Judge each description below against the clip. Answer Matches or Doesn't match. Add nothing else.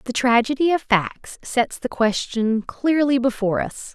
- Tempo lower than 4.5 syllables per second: Matches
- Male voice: Doesn't match